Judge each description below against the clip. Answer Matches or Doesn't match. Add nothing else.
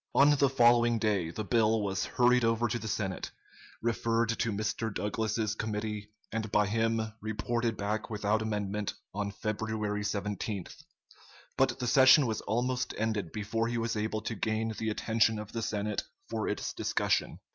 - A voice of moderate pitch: Doesn't match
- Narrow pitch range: Matches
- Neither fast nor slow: Matches